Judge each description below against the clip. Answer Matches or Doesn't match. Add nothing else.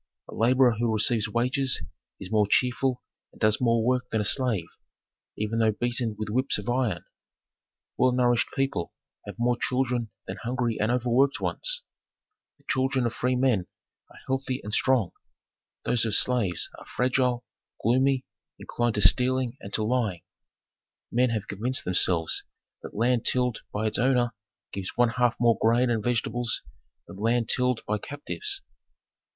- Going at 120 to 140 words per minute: Doesn't match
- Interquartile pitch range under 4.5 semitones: Matches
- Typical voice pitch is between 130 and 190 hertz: Doesn't match